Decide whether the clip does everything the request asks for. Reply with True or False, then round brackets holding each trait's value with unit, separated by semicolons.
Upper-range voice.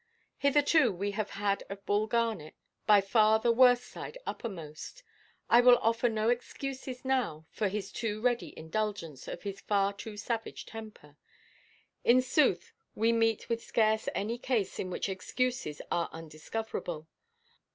True (220 Hz)